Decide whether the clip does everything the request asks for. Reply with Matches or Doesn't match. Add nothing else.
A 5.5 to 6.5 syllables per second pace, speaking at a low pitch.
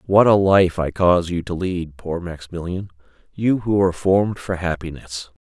Doesn't match